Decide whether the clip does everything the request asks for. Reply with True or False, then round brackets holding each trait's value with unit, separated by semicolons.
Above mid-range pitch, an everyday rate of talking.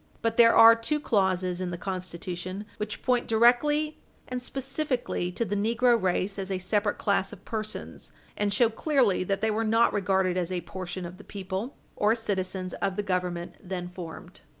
True (200 Hz; 180 wpm)